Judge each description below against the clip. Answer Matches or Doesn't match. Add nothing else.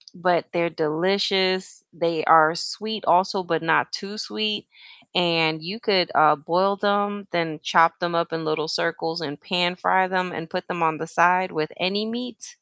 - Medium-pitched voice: Matches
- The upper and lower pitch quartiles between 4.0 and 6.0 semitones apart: Doesn't match